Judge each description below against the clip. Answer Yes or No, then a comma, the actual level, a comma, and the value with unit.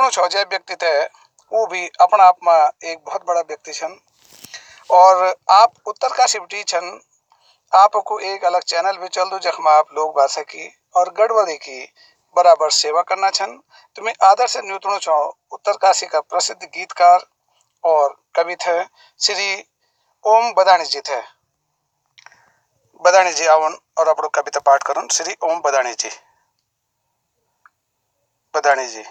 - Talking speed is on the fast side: No, average, 150 wpm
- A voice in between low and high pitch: Yes, medium, 180 Hz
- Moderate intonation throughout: Yes, average, 4.1 semitones